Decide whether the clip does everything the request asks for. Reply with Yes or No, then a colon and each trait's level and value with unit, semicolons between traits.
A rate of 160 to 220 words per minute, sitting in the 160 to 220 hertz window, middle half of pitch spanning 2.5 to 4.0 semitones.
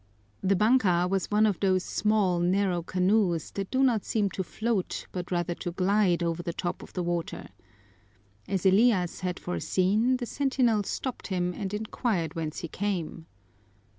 Yes: average, 165 wpm; high, 190 Hz; average, 3.3 semitones